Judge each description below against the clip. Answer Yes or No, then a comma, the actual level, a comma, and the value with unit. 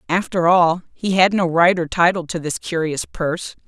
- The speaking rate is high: No, average, 195 wpm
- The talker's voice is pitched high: No, medium, 170 Hz